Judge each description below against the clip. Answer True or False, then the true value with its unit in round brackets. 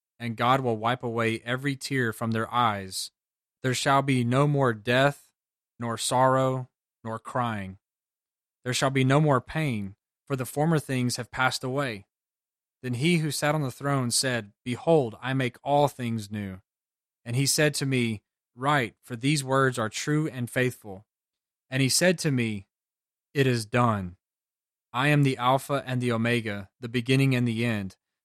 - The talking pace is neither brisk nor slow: True (170 wpm)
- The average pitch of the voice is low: True (125 Hz)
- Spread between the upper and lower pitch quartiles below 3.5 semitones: True (3.0 semitones)